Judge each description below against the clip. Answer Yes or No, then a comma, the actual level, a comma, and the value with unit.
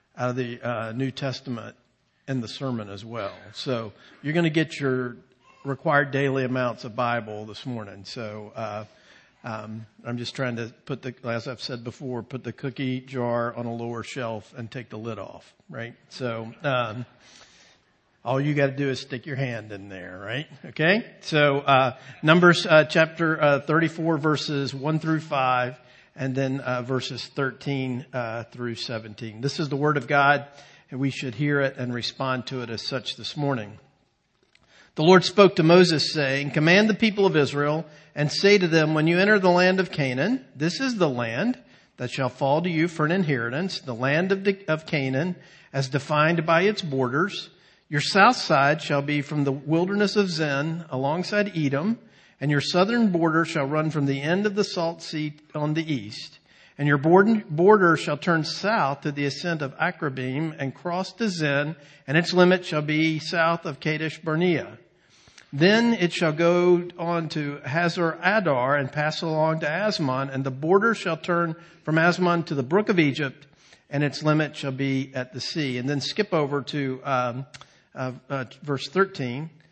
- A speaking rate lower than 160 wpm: No, average, 180 wpm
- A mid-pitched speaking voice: Yes, medium, 145 Hz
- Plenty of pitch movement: No, average, 4.4 semitones